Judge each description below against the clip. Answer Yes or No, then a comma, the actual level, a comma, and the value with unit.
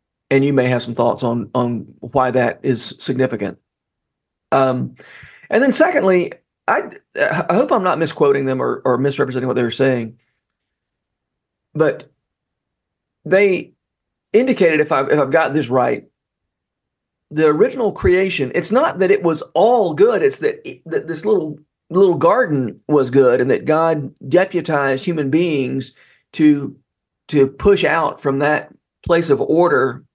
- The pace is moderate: Yes, average, 145 wpm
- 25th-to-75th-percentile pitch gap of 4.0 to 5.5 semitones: Yes, average, 5.2 semitones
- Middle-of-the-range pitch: Yes, medium, 145 Hz